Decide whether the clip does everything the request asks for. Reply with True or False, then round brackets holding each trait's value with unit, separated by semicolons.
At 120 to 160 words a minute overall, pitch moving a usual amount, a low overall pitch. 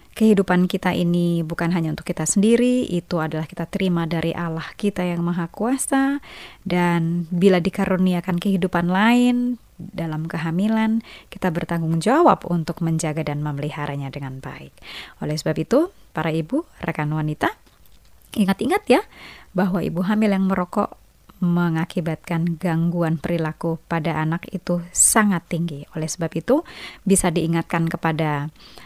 False (130 wpm; 3.0 semitones; 175 Hz)